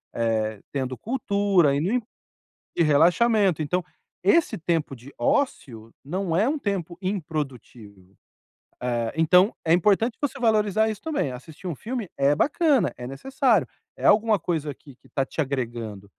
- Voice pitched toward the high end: No, medium, 170 Hz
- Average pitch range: No, wide, 8.0 semitones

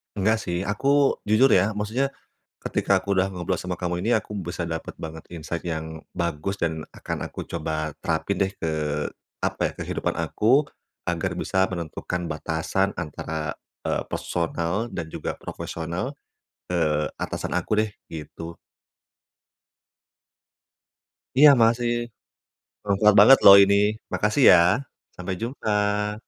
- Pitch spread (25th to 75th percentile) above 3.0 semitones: Yes, average, 4.2 semitones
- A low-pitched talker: Yes, very low, 95 Hz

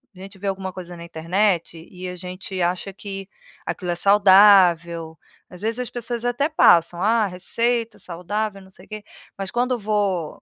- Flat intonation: No, average, 3.1 semitones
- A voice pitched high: Yes, high, 195 Hz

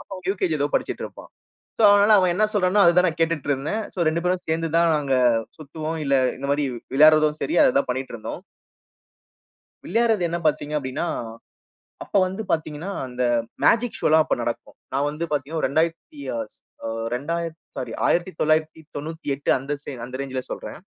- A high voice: No, medium, 155 Hz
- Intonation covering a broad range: No, average, 3.4 semitones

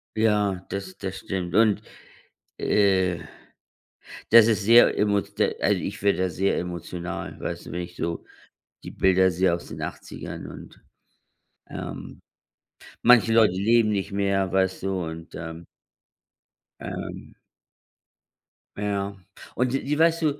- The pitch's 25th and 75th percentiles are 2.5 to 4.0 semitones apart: Yes, average, 2.9 semitones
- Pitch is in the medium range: No, low, 100 Hz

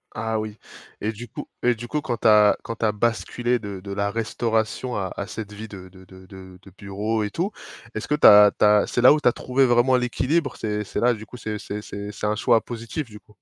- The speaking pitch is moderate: No, low, 110 Hz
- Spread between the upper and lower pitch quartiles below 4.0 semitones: Yes, average, 2.7 semitones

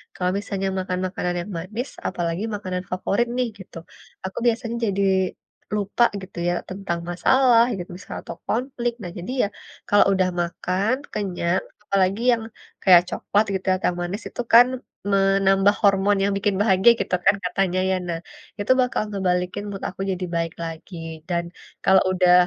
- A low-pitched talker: No, high, 195 Hz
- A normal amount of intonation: No, narrow, 2.2 semitones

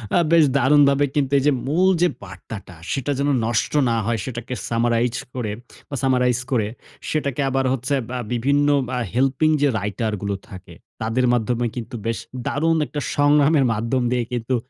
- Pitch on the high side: No, low, 125 Hz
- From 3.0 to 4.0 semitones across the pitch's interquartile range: Yes, average, 3.5 semitones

